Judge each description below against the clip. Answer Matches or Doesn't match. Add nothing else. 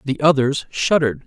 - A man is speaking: Matches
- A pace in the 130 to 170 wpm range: Matches